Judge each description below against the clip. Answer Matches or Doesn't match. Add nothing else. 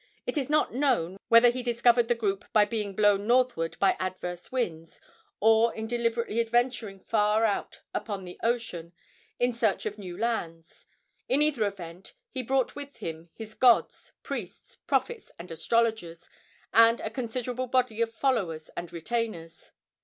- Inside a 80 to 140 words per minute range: Doesn't match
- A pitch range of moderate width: Matches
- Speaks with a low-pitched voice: Doesn't match